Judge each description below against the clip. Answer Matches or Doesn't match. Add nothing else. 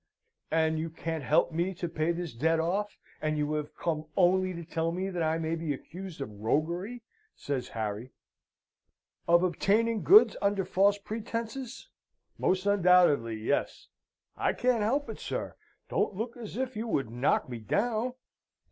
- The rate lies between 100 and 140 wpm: Doesn't match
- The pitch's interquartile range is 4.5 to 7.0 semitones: Matches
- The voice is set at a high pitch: Doesn't match